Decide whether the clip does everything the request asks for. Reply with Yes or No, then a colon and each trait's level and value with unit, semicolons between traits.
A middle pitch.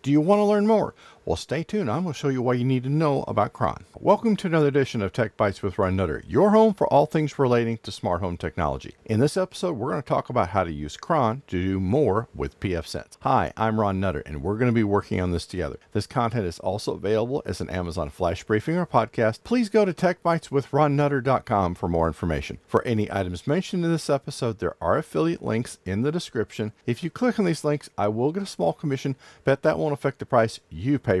No: low, 120 Hz